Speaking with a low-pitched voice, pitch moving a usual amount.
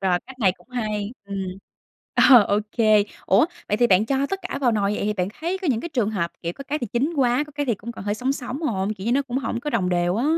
No: high, 235 Hz; average, 4.9 semitones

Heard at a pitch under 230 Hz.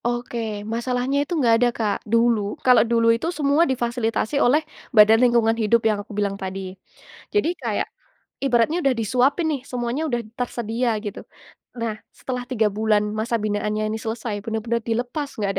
No: high, 235 Hz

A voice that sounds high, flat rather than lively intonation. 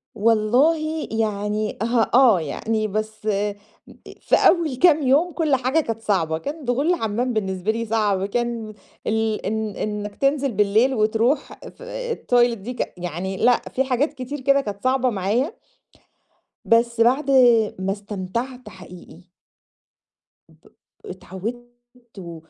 No: high, 230 Hz; average, 4.0 semitones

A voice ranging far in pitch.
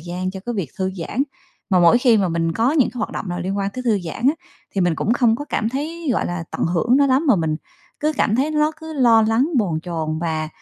Yes: wide, 6.8 semitones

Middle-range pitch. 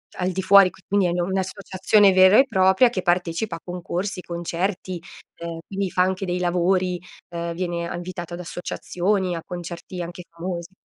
Yes: medium, 180 Hz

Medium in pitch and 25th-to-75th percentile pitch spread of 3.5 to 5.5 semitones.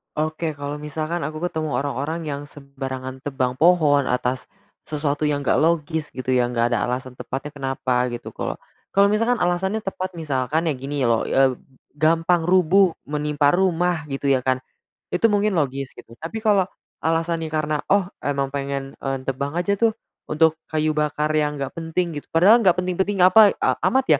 Yes: medium, 155 Hz; average, 4.2 semitones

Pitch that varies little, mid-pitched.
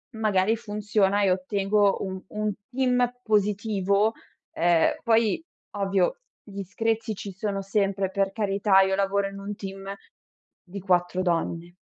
No: narrow, 1.7 semitones; high, 200 Hz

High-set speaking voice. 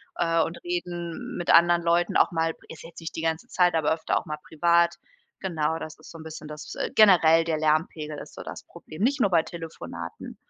No: medium, 165 Hz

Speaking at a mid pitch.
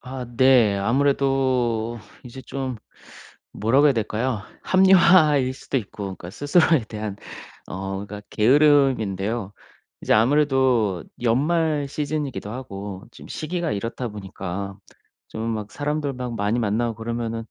No: low, 120 Hz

